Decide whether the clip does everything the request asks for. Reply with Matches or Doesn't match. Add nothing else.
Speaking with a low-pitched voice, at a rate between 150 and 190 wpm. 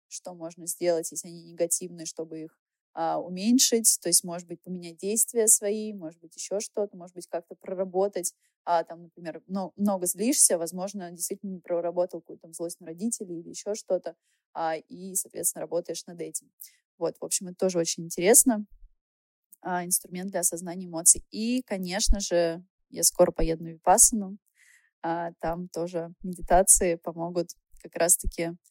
Doesn't match